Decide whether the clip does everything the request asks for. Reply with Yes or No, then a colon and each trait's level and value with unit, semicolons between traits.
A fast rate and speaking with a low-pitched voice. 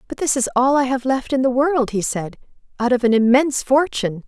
No: fast, 240 wpm; very high, 255 Hz